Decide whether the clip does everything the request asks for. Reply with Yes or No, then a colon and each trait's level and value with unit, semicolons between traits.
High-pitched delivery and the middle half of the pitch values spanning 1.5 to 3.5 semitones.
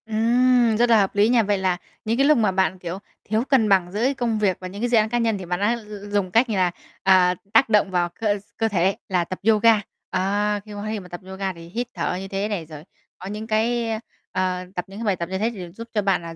Yes: high, 205 Hz; average, 3.2 semitones